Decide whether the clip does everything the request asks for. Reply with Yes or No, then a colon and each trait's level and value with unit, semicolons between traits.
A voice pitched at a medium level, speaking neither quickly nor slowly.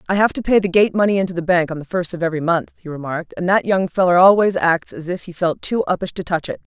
No: medium, 180 Hz; fast, 295 wpm